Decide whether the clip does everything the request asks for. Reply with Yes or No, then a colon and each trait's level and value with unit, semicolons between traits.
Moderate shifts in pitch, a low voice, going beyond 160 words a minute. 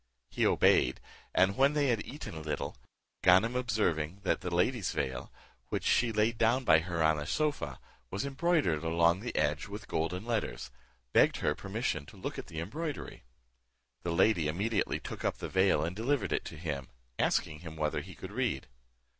No: wide, 6.5 semitones; very low, 95 Hz; average, 180 wpm